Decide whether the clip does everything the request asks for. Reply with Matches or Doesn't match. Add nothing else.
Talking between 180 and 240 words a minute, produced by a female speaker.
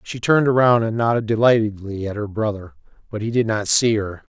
Doesn't match